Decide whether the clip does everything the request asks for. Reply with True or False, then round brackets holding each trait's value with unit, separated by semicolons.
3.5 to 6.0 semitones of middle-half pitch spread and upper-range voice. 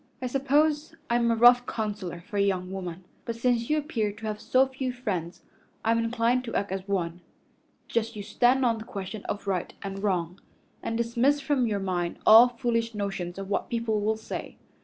True (3.8 semitones; 225 Hz)